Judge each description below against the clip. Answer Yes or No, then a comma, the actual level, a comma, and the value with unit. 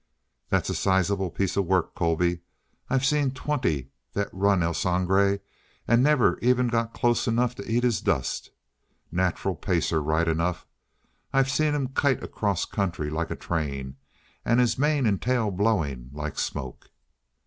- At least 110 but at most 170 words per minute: Yes, average, 155 wpm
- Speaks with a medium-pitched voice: No, low, 100 Hz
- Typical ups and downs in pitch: No, wide, 6.6 semitones